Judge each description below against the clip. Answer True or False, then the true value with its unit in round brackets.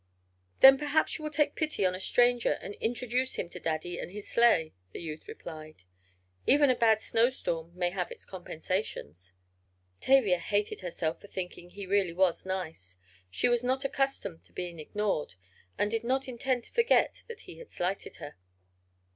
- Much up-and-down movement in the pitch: True (6.6 semitones)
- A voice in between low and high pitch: False (200 Hz)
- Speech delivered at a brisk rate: False (170 wpm)